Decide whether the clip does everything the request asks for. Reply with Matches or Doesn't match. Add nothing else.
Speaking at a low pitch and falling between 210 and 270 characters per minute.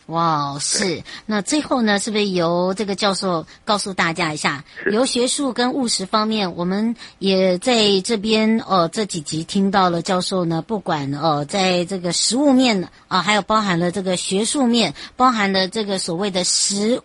Doesn't match